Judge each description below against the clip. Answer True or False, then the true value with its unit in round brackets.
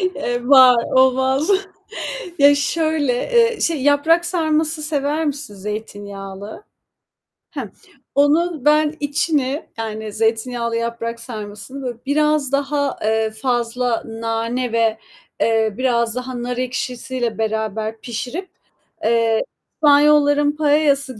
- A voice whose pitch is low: False (255 Hz)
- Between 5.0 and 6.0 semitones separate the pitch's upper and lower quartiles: False (4.4 semitones)